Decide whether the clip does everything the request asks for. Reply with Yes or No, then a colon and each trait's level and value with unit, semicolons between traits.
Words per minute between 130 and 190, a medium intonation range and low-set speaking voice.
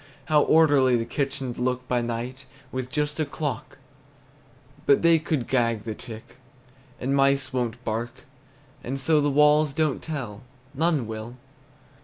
Yes: average, 150 wpm; average, 3.6 semitones; low, 130 Hz